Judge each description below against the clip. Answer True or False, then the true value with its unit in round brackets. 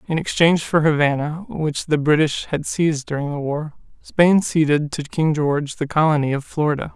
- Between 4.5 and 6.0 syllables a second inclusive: True (5.3 syllables/s)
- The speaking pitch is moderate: True (150 Hz)